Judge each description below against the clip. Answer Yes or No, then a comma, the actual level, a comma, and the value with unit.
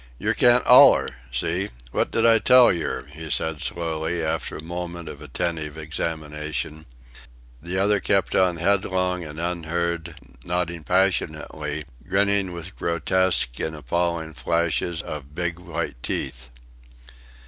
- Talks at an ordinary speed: No, slow, 125 wpm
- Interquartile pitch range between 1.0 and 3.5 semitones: Yes, narrow, 2.4 semitones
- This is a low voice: Yes, very low, 85 Hz